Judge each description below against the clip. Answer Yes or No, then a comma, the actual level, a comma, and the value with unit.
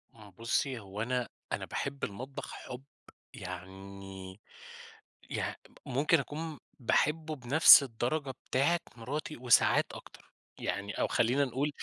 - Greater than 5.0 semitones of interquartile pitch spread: Yes, wide, 5.6 semitones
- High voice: No, low, 125 Hz